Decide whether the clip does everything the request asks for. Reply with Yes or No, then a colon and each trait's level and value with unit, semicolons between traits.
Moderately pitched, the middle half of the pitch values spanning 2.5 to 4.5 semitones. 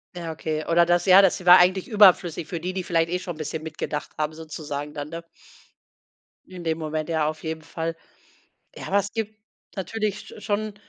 Yes: medium, 170 Hz; average, 2.9 semitones